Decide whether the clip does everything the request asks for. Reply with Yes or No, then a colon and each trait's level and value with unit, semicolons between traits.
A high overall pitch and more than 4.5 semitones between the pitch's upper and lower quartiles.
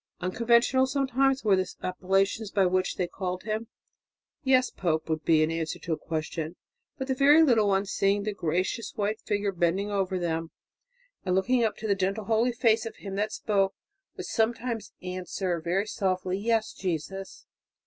No: high, 200 Hz; average, 3.7 semitones